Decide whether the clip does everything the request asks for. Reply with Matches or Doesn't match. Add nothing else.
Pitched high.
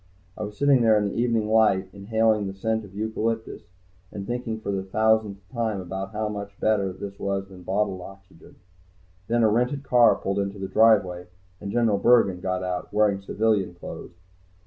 Doesn't match